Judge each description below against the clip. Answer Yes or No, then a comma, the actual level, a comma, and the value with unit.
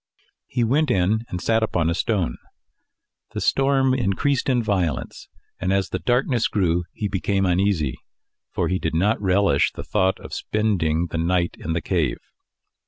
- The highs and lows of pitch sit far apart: No, average, 4.6 semitones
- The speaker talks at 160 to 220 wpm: Yes, average, 165 wpm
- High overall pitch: No, very low, 95 Hz